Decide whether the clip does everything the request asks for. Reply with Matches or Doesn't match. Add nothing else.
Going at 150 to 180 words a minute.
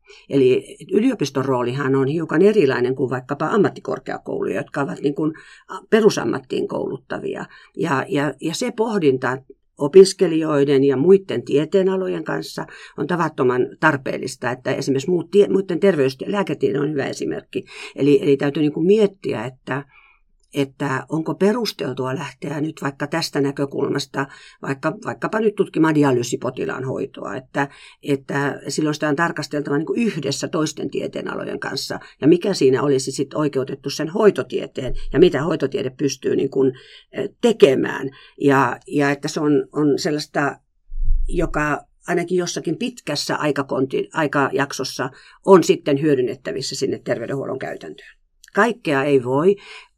Doesn't match